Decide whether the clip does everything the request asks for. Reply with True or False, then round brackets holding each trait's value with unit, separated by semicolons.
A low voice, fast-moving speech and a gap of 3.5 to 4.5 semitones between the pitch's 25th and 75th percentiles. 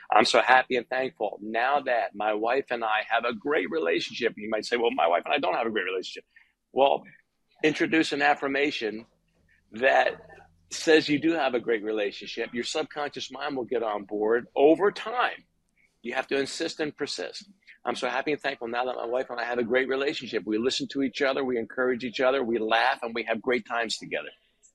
True (130 Hz; 210 wpm; 3.8 semitones)